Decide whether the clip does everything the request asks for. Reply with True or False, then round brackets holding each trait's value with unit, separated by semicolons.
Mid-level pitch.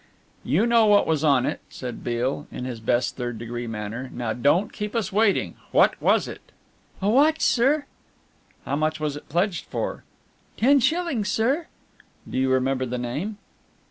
True (150 Hz)